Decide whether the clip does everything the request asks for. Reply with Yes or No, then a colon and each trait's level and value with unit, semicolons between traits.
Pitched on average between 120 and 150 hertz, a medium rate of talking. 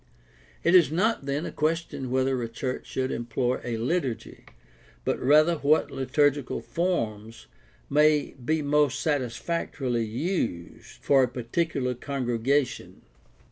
No: low, 135 Hz; slow, 120 wpm